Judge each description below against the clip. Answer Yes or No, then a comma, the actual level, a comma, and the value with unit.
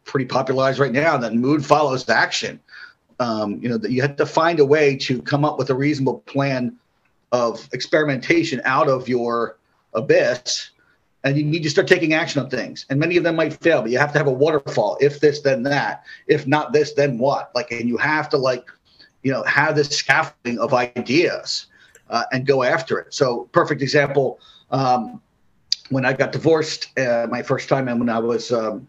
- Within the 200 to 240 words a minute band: Yes, fast, 205 wpm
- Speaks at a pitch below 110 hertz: No, low, 135 Hz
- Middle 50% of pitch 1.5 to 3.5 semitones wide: Yes, average, 3.2 semitones